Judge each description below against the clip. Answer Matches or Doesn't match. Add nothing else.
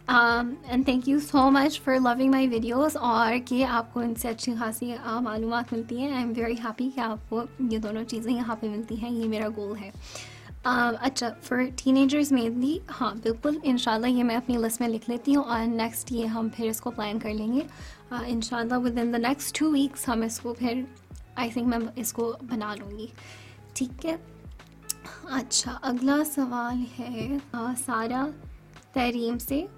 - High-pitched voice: Matches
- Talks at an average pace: Doesn't match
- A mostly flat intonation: Matches